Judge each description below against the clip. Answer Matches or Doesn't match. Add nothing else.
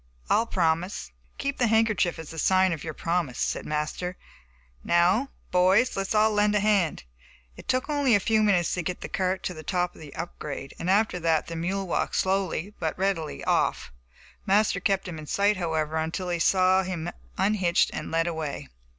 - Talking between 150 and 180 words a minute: Doesn't match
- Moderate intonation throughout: Matches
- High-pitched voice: Doesn't match